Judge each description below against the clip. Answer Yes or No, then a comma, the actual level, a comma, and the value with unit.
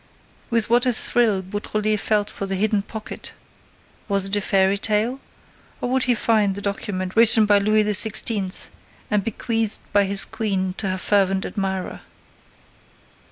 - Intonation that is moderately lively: No, narrow, 2.1 semitones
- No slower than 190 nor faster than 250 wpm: No, average, 155 wpm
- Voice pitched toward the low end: No, high, 205 Hz